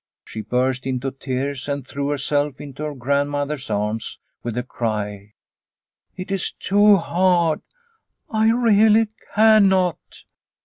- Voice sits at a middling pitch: Yes, medium, 145 Hz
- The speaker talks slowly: Yes, slow, 120 wpm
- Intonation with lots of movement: Yes, wide, 6.7 semitones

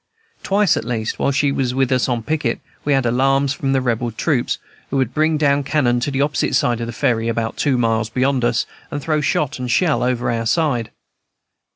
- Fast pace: Yes, fast, 220 wpm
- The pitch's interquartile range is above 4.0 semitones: No, average, 3.2 semitones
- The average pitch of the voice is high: No, low, 130 Hz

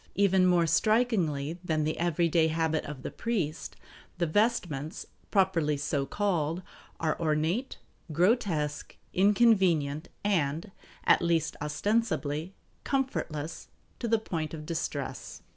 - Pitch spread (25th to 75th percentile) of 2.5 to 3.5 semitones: No, average, 4.7 semitones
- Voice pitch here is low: No, medium, 170 Hz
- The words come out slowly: Yes, slow, 110 wpm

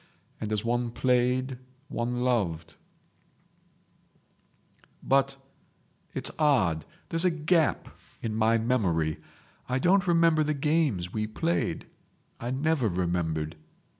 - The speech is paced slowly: Yes, slow, 100 wpm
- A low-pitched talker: Yes, low, 125 Hz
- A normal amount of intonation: No, wide, 6.3 semitones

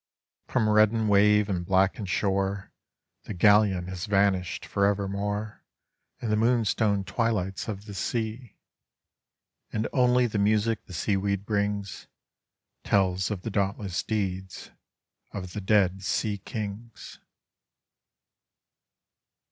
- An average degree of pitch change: No, narrow, 2.0 semitones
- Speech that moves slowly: Yes, slow, 110 wpm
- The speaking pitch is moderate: No, low, 100 Hz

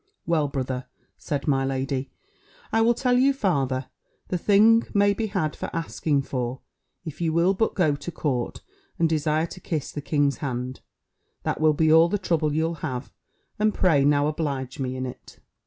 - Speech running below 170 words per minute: No, average, 180 wpm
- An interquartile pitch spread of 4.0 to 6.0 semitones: Yes, average, 4.4 semitones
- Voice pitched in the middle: Yes, medium, 155 Hz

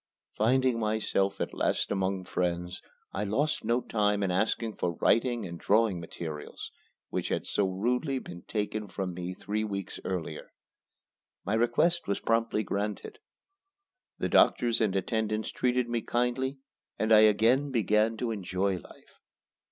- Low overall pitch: Yes, low, 110 Hz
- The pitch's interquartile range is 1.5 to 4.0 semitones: Yes, average, 3.6 semitones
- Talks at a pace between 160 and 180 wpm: No, average, 145 wpm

